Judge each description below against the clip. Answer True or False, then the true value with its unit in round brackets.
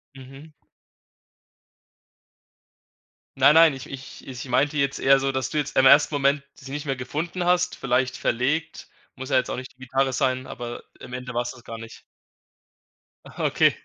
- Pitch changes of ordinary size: False (2.1 semitones)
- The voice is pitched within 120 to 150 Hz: True (135 Hz)